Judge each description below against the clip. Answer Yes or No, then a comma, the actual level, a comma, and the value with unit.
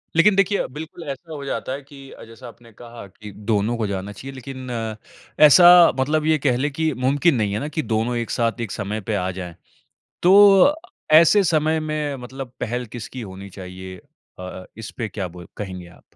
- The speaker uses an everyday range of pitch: No, wide, 6.7 semitones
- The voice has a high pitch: No, low, 125 Hz